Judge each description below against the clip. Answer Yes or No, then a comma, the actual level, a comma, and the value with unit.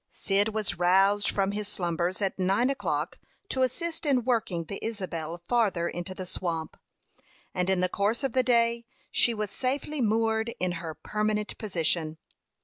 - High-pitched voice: Yes, high, 205 Hz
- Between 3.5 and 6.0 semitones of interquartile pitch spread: Yes, average, 4.4 semitones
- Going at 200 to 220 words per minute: No, average, 160 wpm